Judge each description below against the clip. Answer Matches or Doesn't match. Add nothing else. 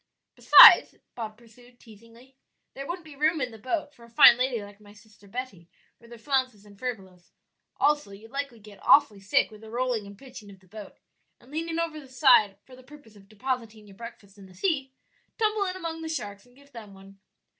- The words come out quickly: Matches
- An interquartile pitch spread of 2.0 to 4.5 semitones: Doesn't match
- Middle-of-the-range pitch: Doesn't match